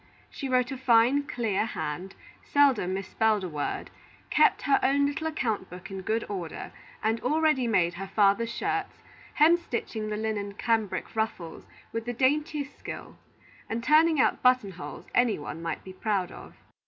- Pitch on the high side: Yes, high, 225 Hz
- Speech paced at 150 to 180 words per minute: Yes, average, 160 wpm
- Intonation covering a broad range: Yes, wide, 5.7 semitones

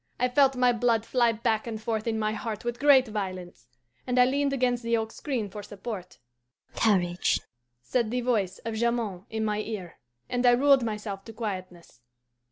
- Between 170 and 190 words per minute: Yes, average, 180 wpm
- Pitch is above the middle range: Yes, high, 225 Hz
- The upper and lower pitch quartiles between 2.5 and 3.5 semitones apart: Yes, average, 2.9 semitones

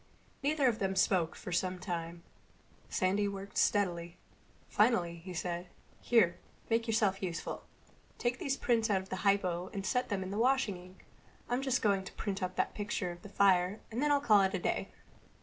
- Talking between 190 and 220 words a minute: Yes, average, 195 wpm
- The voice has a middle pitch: No, high, 195 Hz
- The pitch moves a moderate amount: Yes, average, 3.7 semitones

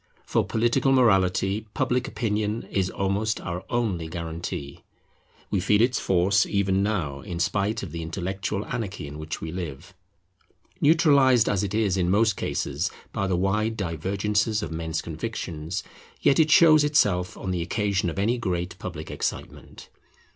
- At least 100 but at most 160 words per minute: Yes, average, 155 wpm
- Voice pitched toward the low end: Yes, low, 100 Hz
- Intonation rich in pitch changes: No, average, 3.8 semitones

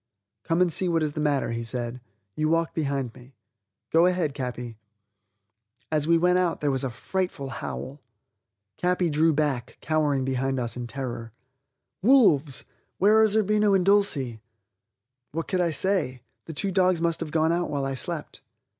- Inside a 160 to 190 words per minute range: Yes, average, 170 wpm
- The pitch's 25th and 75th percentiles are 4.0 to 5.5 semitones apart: Yes, average, 5.1 semitones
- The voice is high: No, medium, 155 Hz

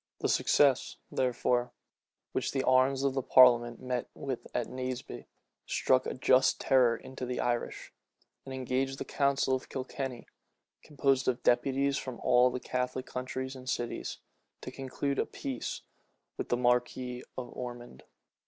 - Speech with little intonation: Yes, narrow, 1.2 semitones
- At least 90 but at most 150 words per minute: Yes, average, 145 wpm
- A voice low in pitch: Yes, low, 130 Hz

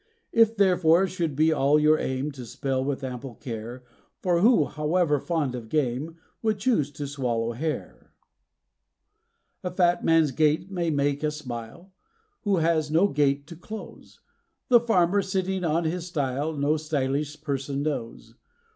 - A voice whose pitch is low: No, medium, 155 Hz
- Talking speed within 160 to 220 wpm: No, average, 150 wpm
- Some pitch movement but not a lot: Yes, average, 4.1 semitones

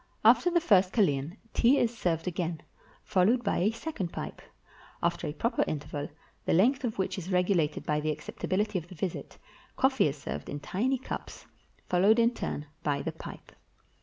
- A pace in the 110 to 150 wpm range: No, average, 175 wpm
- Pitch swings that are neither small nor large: No, wide, 6.5 semitones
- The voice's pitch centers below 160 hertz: No, medium, 185 Hz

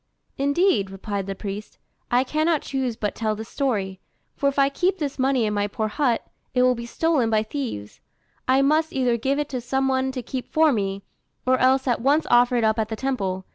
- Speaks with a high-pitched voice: Yes, very high, 250 Hz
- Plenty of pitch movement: No, average, 4.2 semitones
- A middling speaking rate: No, fast, 215 wpm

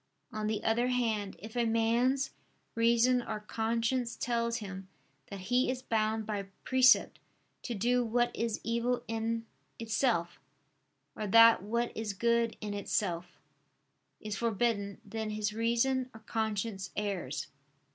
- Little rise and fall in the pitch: Yes, narrow, 2.0 semitones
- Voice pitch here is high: Yes, high, 225 Hz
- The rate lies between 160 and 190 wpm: No, slow, 135 wpm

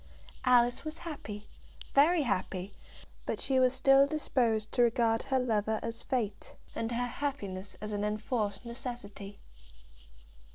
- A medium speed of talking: No, slow, 130 wpm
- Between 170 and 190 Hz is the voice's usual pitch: No, high, 235 Hz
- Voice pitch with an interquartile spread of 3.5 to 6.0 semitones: Yes, average, 3.9 semitones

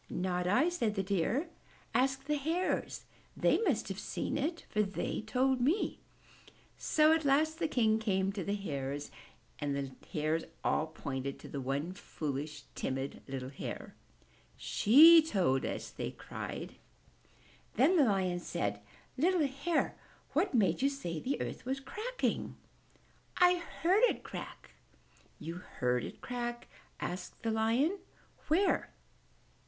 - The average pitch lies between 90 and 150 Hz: No, high, 220 Hz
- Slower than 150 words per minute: Yes, average, 140 wpm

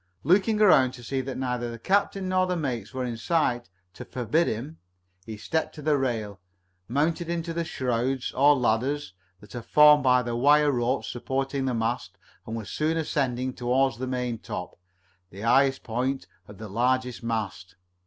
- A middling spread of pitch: Yes, average, 3.8 semitones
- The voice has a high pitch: No, low, 130 Hz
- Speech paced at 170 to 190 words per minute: Yes, average, 175 wpm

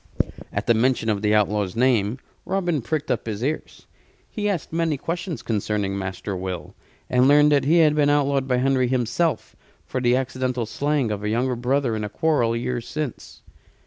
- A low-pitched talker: Yes, low, 125 Hz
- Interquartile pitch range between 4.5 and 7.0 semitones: Yes, average, 5.0 semitones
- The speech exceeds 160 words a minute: Yes, average, 180 wpm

